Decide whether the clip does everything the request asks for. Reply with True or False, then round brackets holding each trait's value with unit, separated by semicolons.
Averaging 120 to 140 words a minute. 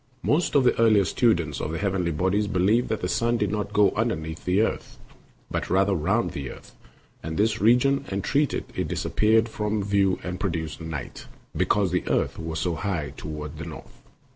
False (190 wpm)